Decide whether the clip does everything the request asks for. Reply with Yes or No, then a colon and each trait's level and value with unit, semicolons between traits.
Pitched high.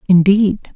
Yes: high, 195 Hz